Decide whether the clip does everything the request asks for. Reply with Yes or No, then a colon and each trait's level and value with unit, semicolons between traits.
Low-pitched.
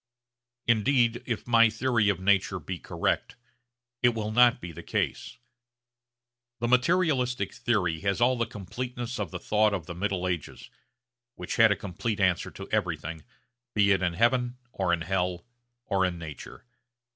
Yes: low, 105 Hz